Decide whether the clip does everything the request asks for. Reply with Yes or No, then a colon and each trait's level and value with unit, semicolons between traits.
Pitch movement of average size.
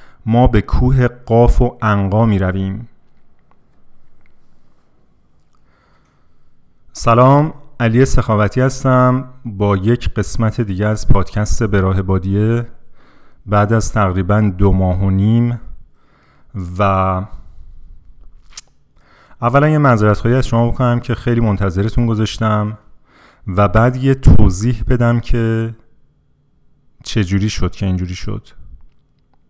Yes: average, 3.7 semitones